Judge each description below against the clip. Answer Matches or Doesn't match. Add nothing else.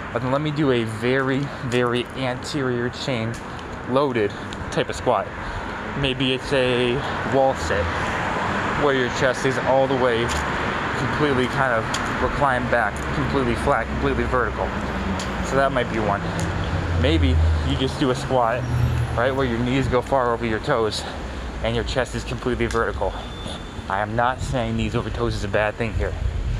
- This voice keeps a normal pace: Matches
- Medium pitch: Doesn't match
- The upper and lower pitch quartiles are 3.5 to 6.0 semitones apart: Matches